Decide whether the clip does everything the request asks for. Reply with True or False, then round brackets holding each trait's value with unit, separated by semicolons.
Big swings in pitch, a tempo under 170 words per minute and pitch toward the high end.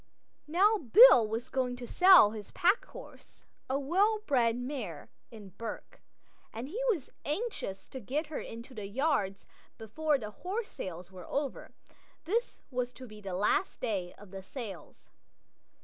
True (7.2 semitones; 150 wpm; 250 Hz)